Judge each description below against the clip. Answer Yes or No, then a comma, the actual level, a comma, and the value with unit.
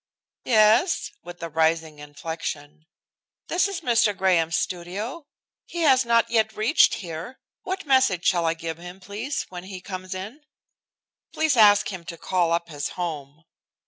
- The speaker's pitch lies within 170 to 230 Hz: Yes, medium, 185 Hz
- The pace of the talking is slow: No, average, 150 wpm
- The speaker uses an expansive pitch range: Yes, wide, 5.8 semitones